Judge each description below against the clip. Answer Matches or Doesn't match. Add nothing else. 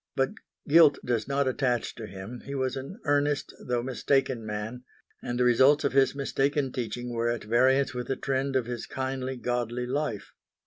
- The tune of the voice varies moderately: Doesn't match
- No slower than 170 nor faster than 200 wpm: Matches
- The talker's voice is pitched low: Matches